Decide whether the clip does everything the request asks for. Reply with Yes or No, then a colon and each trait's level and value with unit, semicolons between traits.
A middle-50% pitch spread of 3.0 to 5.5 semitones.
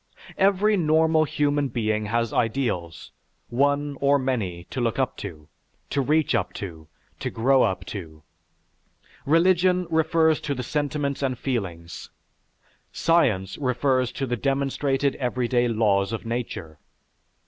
Yes: average, 5.1 semitones